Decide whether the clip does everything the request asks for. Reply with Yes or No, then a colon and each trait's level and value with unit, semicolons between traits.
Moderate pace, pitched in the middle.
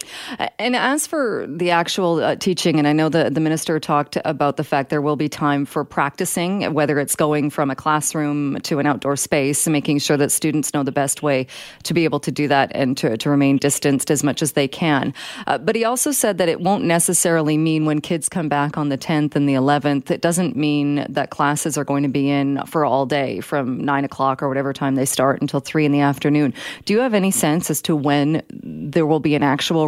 No: fast, 235 wpm; medium, 150 Hz